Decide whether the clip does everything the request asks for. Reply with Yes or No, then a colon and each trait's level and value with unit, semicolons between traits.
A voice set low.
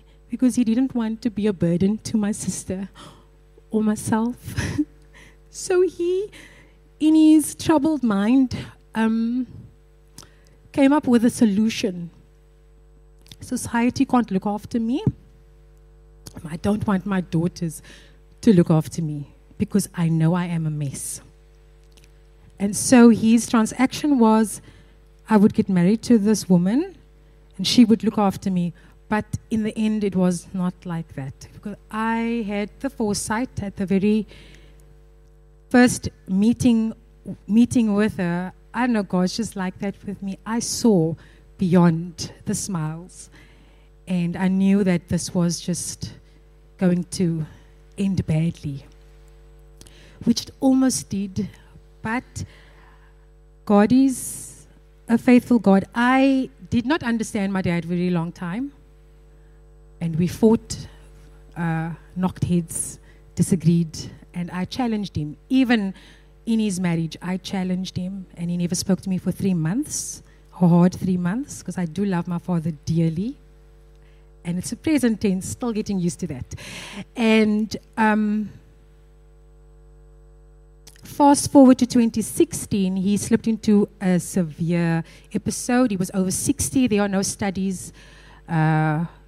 No: medium, 185 Hz